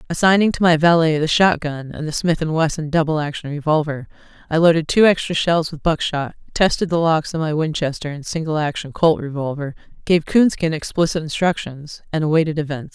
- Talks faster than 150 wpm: Yes, average, 185 wpm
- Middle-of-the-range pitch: Yes, medium, 160 Hz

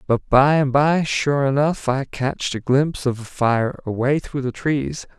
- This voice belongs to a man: Yes, male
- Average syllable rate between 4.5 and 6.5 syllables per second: No, 4.1 syllables/s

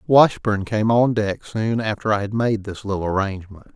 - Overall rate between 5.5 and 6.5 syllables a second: No, 5.1 syllables/s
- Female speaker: No, male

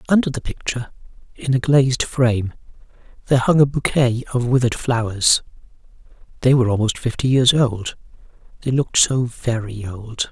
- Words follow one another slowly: No, average, 145 wpm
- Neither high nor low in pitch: No, low, 125 Hz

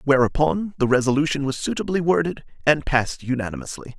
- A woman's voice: No, male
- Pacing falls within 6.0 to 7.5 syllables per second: Yes, 6.1 syllables/s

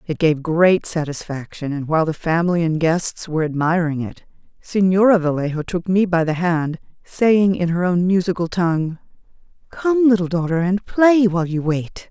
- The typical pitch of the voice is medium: Yes, medium, 175 Hz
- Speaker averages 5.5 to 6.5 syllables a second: No, 5.0 syllables/s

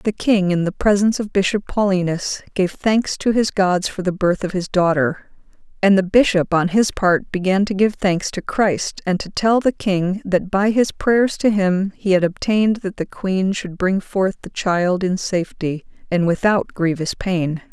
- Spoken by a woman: Yes, female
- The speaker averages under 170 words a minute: No, average, 200 wpm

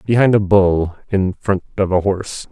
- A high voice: No, very low, 95 Hz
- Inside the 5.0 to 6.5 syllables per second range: No, 4.8 syllables/s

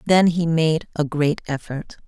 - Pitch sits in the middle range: Yes, medium, 160 Hz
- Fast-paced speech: No, average, 175 wpm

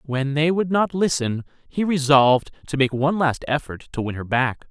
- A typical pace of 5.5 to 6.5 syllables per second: No, 5.0 syllables/s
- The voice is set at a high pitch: No, medium, 145 Hz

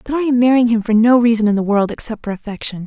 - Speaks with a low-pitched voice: No, high, 230 Hz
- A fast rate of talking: Yes, fast, 275 wpm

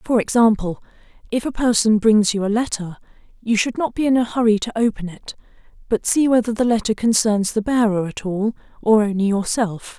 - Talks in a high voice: Yes, high, 220 Hz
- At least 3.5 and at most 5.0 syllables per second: No, 5.4 syllables/s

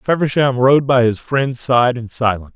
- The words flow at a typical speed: Yes, average, 190 wpm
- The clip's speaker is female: No, male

